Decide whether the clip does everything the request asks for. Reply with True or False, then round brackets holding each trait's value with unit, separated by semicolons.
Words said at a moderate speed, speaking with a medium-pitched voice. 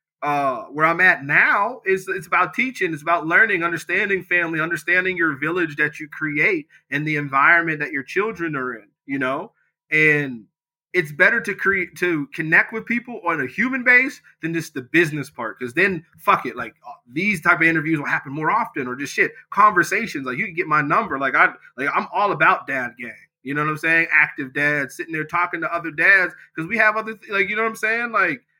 False (215 wpm; 165 Hz)